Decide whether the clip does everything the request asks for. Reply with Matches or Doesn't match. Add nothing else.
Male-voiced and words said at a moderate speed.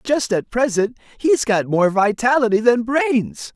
Matches